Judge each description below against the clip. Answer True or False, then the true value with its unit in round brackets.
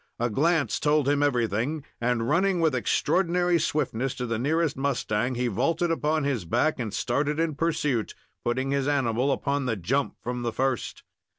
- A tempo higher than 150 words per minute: True (170 wpm)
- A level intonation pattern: False (4.2 semitones)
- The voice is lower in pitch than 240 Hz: True (135 Hz)